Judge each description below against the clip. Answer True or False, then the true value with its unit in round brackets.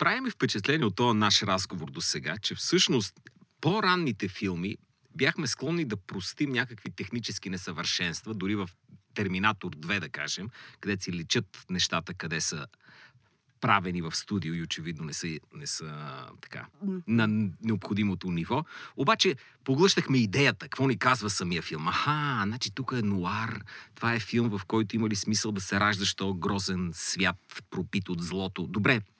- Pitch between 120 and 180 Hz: False (105 Hz)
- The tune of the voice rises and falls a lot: False (4.9 semitones)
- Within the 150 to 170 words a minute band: True (155 wpm)